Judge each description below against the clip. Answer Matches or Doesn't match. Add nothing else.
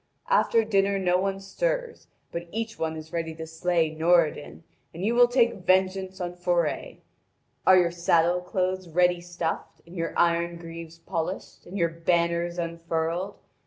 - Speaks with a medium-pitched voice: Matches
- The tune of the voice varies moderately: Doesn't match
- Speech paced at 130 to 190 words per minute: Matches